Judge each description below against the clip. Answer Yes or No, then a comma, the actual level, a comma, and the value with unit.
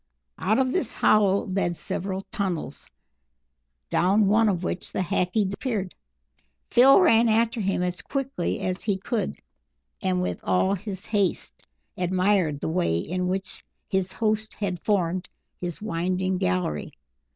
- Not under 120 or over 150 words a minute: Yes, average, 140 wpm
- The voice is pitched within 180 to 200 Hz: Yes, high, 190 Hz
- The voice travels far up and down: No, average, 2.9 semitones